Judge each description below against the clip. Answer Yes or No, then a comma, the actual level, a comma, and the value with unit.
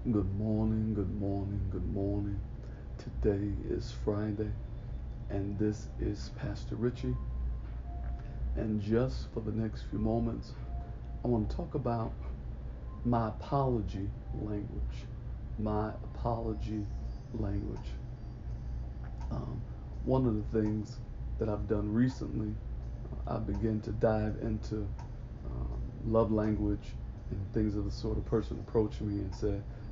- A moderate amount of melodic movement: No, narrow, 2.2 semitones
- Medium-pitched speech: No, low, 105 Hz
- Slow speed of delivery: Yes, slow, 120 wpm